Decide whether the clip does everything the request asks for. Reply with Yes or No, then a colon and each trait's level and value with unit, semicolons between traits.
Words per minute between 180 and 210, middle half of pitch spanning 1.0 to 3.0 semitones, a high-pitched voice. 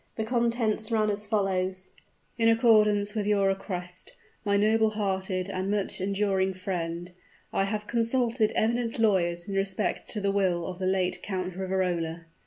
No: average, 160 wpm; narrow, 2.5 semitones; high, 200 Hz